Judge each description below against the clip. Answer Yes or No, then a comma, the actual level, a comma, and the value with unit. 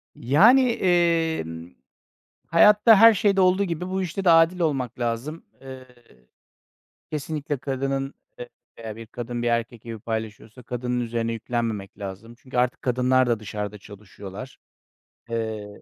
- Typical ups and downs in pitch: No, wide, 6.4 semitones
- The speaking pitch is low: Yes, low, 125 Hz